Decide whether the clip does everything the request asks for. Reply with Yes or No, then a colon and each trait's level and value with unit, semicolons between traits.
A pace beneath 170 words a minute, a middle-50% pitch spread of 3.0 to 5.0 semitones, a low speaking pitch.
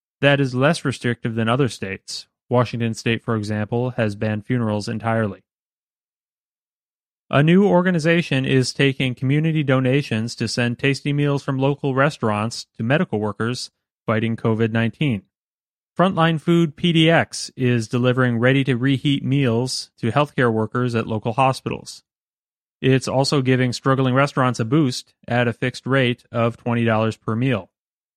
Yes: average, 140 wpm; average, 3.3 semitones; low, 125 Hz